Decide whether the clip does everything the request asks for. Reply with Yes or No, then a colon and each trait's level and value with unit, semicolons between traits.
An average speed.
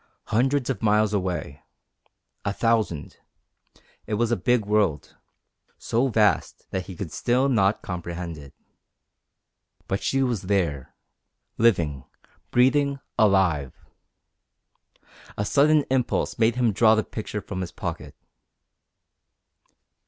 No: slow, 115 wpm